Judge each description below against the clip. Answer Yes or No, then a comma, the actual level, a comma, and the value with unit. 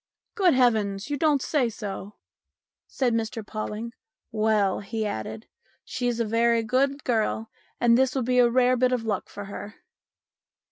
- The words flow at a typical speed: Yes, average, 170 wpm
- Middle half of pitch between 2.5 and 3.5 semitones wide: Yes, average, 2.9 semitones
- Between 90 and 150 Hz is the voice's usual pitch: No, high, 230 Hz